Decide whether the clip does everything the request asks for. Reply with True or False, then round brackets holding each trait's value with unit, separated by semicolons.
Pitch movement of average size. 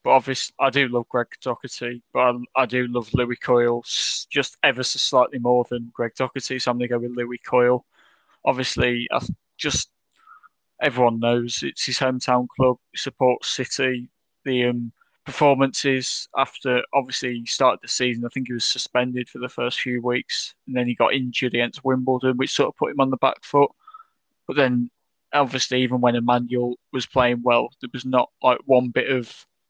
False (1.3 semitones)